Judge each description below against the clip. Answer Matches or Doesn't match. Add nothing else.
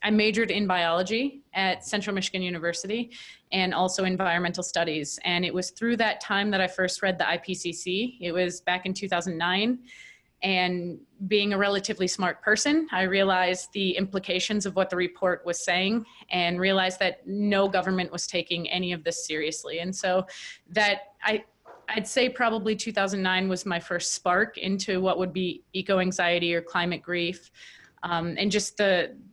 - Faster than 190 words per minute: Doesn't match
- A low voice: Doesn't match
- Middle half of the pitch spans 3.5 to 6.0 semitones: Doesn't match